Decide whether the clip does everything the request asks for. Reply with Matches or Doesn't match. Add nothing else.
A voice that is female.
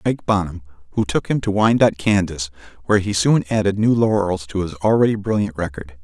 Doesn't match